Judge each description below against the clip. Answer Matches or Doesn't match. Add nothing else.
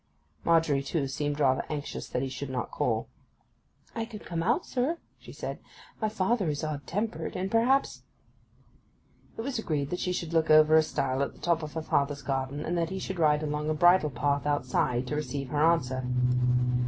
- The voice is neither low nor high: Matches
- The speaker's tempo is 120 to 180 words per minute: Doesn't match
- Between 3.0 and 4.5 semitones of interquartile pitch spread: Matches